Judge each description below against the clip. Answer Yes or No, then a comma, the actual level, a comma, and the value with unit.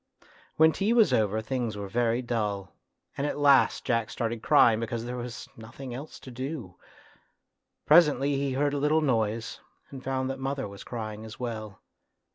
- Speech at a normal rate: Yes, average, 170 wpm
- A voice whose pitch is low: Yes, low, 120 Hz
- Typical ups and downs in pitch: Yes, average, 3.9 semitones